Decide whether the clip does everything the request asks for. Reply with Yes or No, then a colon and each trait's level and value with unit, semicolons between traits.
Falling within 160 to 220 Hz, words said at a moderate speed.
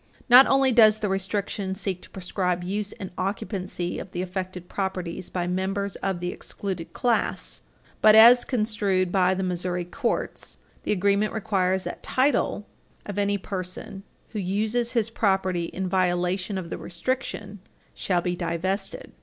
Yes: high, 190 Hz; average, 150 wpm